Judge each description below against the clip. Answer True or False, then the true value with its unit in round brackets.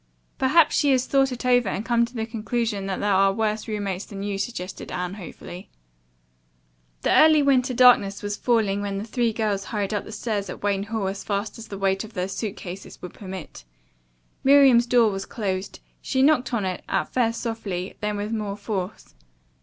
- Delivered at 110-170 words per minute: False (195 wpm)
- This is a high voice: True (210 Hz)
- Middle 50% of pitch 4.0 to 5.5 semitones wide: False (3.3 semitones)